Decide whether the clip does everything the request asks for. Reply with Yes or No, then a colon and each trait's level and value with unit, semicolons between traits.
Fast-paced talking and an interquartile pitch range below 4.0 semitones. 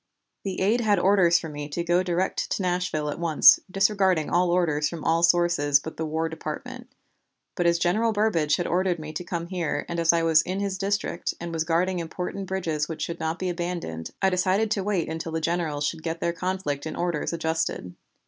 Yes: fast, 210 wpm; narrow, 2.5 semitones